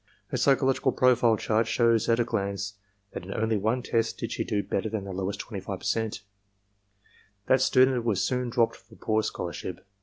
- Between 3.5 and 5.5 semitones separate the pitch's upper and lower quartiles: No, average, 3.1 semitones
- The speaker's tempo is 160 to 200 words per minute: Yes, average, 175 wpm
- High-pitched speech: No, low, 110 Hz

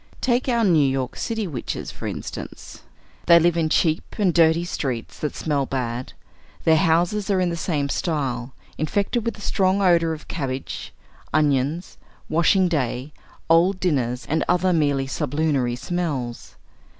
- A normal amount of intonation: Yes, average, 4.6 semitones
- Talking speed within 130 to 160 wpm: Yes, average, 150 wpm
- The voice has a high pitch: No, medium, 160 Hz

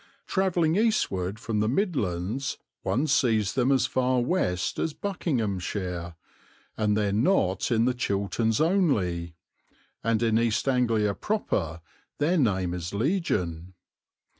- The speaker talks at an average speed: No, slow, 120 wpm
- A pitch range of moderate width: No, wide, 6.7 semitones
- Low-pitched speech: Yes, low, 115 Hz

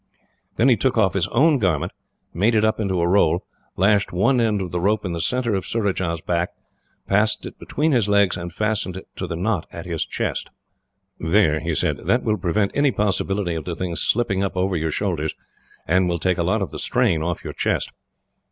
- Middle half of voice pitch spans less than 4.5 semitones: Yes, average, 3.9 semitones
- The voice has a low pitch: Yes, very low, 95 Hz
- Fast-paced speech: Yes, fast, 215 wpm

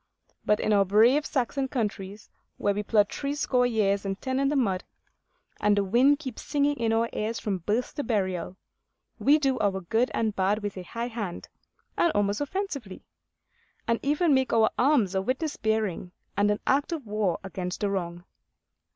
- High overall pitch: Yes, high, 220 Hz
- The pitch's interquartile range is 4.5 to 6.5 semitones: Yes, average, 5.0 semitones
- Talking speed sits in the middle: Yes, average, 180 wpm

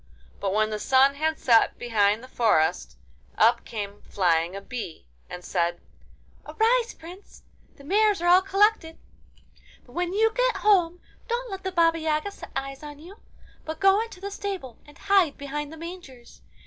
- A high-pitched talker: Yes, very high, 315 Hz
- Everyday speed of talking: Yes, average, 170 wpm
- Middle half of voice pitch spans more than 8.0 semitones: Yes, wide, 8.7 semitones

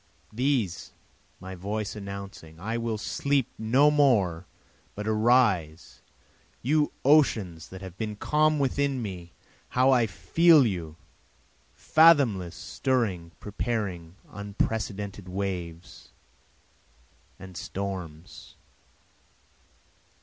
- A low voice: Yes, low, 105 Hz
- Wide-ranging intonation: Yes, wide, 5.8 semitones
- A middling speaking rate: No, slow, 90 wpm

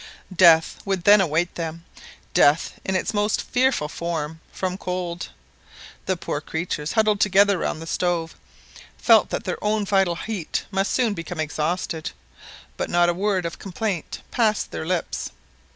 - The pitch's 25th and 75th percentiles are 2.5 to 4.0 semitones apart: Yes, average, 3.4 semitones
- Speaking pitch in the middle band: Yes, medium, 180 Hz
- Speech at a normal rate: Yes, average, 150 wpm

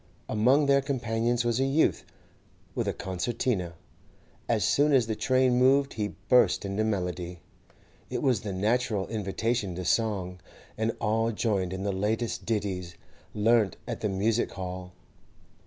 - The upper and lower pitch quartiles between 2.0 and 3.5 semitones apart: No, average, 4.1 semitones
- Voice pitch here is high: No, low, 110 Hz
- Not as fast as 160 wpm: Yes, average, 145 wpm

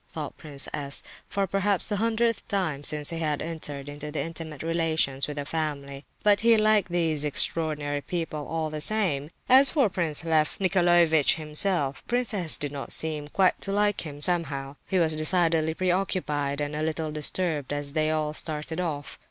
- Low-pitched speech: No, medium, 160 Hz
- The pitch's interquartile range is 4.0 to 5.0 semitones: No, average, 3.6 semitones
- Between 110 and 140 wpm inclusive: No, average, 170 wpm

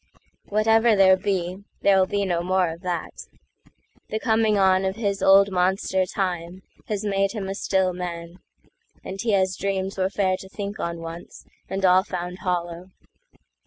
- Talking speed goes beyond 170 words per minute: No, average, 150 wpm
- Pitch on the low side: No, high, 190 Hz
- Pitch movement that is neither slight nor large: No, narrow, 1.6 semitones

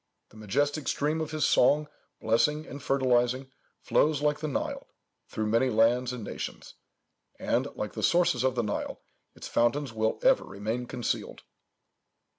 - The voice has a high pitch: No, low, 130 Hz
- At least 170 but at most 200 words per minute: No, average, 150 wpm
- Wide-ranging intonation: No, average, 4.4 semitones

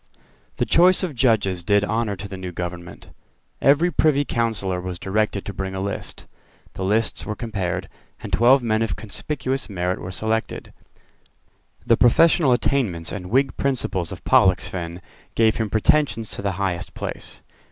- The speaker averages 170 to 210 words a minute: No, average, 155 wpm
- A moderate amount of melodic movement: Yes, average, 4.5 semitones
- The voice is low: Yes, low, 105 Hz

